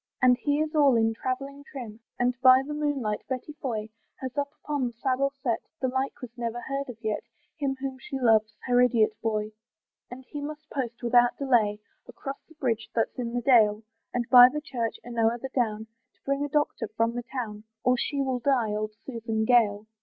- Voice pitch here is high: Yes, high, 245 Hz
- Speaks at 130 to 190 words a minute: No, fast, 205 wpm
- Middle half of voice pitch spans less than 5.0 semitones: Yes, average, 3.2 semitones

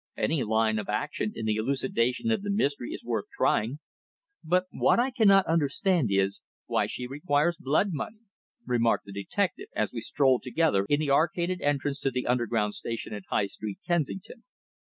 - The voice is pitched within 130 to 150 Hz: Yes, medium, 140 Hz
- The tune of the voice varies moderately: No, wide, 7.4 semitones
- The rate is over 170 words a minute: Yes, average, 180 wpm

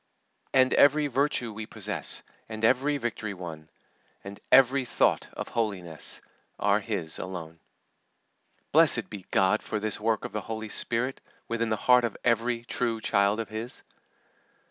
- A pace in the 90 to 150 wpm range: Yes, average, 145 wpm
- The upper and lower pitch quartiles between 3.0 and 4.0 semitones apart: Yes, average, 3.4 semitones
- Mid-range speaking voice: No, low, 110 Hz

